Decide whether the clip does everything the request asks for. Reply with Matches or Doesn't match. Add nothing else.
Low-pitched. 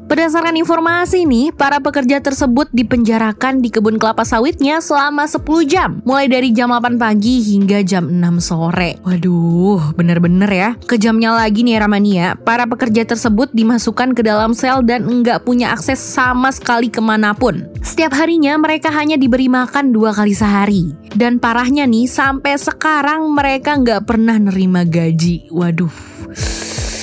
Doesn't match